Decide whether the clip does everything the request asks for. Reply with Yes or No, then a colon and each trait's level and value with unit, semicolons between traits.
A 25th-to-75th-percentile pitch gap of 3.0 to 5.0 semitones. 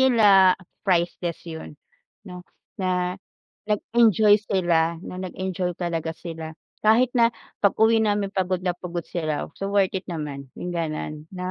Yes: average, 3.4 semitones